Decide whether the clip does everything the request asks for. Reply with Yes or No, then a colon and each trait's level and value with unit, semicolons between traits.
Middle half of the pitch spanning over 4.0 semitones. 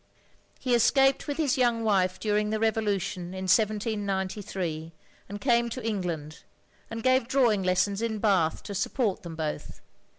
No: average, 3.6 semitones